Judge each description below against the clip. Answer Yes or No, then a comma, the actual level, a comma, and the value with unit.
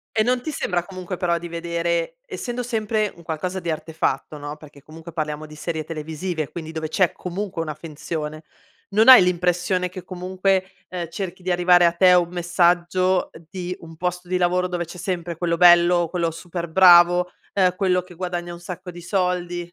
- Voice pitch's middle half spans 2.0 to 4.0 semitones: No, narrow, 1.6 semitones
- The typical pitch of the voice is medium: Yes, medium, 175 Hz